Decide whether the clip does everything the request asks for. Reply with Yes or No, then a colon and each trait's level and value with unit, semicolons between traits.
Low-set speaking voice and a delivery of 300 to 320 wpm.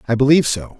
No: low, 130 Hz; fast, 225 wpm